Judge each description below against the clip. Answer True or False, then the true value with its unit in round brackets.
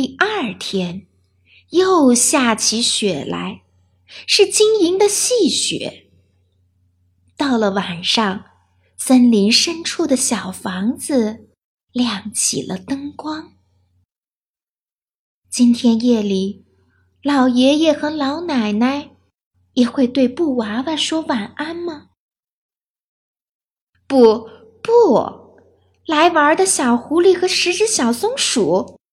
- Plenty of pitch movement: True (8.3 semitones)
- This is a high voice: True (245 Hz)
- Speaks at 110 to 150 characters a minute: True (135 characters per minute)